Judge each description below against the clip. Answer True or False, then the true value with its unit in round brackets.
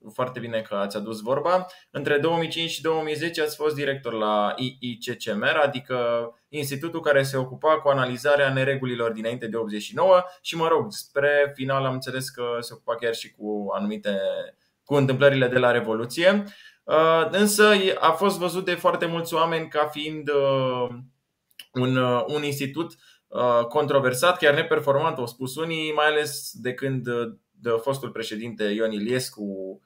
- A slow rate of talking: False (145 wpm)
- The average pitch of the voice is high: False (140 Hz)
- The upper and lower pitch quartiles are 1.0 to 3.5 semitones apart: False (4.9 semitones)